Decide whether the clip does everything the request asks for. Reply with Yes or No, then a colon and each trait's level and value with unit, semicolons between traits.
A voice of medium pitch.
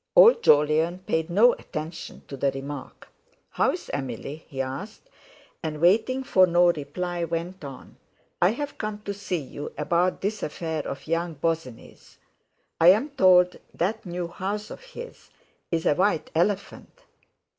Yes: medium, 175 Hz